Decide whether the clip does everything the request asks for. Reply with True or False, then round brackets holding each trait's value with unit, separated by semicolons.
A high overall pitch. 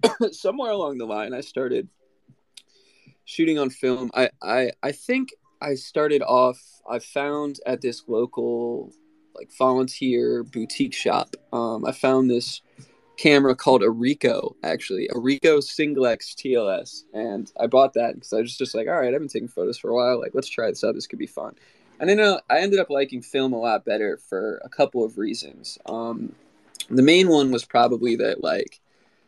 False (135 Hz)